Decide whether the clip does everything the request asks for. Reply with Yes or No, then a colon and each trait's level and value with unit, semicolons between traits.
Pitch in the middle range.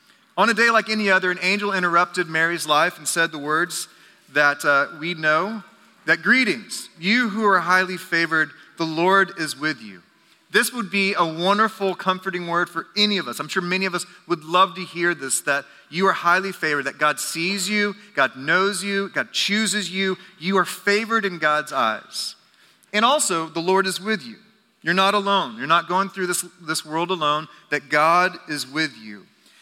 Yes: medium, 180 Hz